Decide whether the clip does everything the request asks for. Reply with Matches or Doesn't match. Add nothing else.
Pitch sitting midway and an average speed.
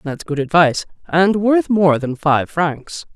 Matches